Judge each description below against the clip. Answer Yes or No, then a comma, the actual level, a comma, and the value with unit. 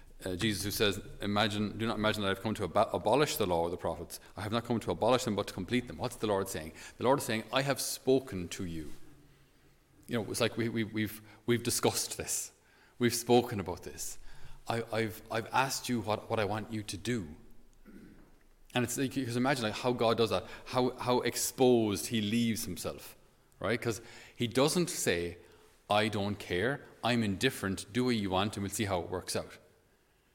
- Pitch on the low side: Yes, low, 110 Hz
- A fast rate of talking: Yes, fast, 220 wpm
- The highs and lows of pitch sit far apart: No, average, 3.3 semitones